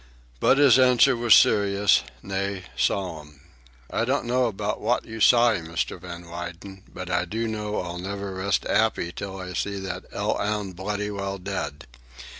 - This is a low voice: Yes, low, 100 Hz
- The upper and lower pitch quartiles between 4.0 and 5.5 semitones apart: No, average, 3.2 semitones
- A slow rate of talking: No, average, 165 wpm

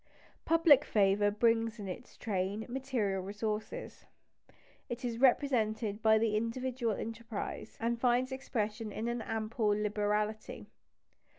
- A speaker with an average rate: No, slow, 110 wpm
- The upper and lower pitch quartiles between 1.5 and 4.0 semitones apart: Yes, narrow, 2.4 semitones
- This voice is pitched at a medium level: No, high, 225 Hz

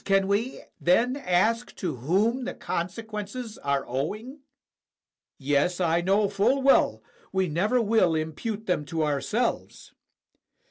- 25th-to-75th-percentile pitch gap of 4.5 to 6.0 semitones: Yes, wide, 5.6 semitones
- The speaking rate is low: Yes, slow, 130 wpm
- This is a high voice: Yes, high, 195 Hz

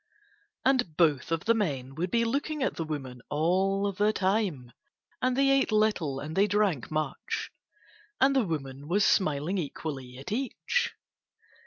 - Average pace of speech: Yes, average, 155 wpm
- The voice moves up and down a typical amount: No, wide, 6.8 semitones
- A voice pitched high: No, medium, 180 Hz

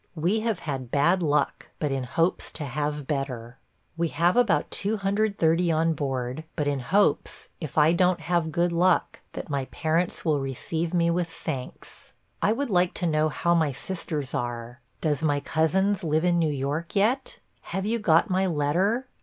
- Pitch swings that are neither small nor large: Yes, average, 4.0 semitones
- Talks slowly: No, average, 175 wpm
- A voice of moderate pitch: Yes, medium, 165 Hz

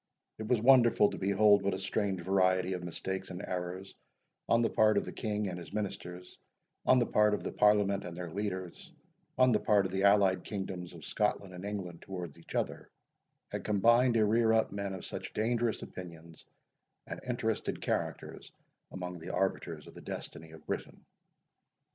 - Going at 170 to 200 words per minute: Yes, average, 180 wpm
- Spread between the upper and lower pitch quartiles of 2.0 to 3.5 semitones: Yes, average, 2.9 semitones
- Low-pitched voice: Yes, very low, 95 Hz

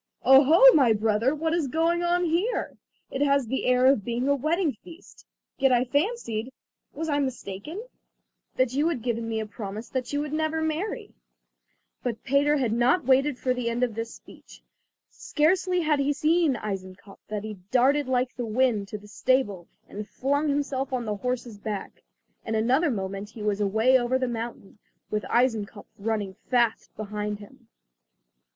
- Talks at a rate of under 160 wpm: No, average, 170 wpm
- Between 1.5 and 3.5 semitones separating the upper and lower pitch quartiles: No, average, 5.0 semitones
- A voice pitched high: Yes, very high, 255 Hz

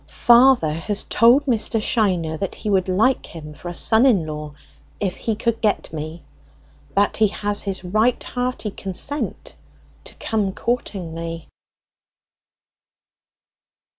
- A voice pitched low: No, high, 205 Hz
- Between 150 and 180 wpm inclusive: No, slow, 135 wpm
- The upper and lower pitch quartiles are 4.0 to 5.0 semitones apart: No, wide, 5.5 semitones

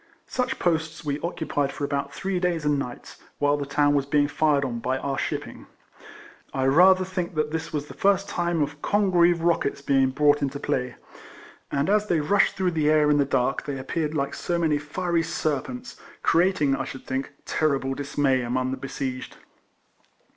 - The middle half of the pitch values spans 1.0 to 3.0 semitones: No, average, 3.6 semitones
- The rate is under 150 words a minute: No, average, 185 wpm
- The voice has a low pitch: No, medium, 150 Hz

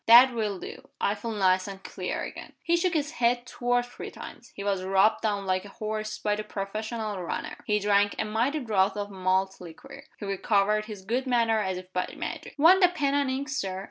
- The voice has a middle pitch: No, high, 215 Hz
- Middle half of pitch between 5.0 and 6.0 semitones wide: No, average, 3.8 semitones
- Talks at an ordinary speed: No, fast, 220 wpm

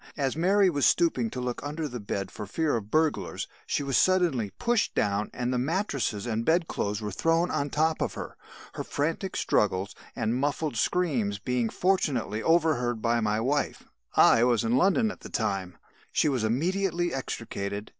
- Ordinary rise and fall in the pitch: No, wide, 6.7 semitones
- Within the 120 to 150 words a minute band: No, average, 175 wpm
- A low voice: Yes, low, 130 Hz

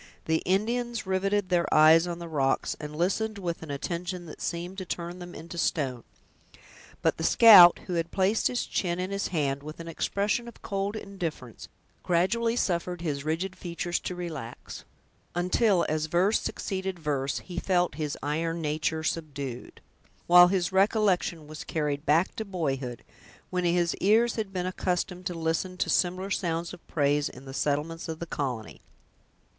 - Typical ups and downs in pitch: Yes, average, 3.3 semitones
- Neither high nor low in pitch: Yes, medium, 175 Hz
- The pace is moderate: Yes, average, 165 wpm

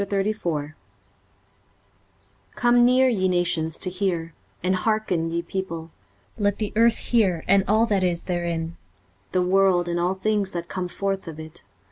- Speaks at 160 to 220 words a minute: No, average, 150 wpm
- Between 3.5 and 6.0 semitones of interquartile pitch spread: No, average, 3.0 semitones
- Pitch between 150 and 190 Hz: Yes, medium, 185 Hz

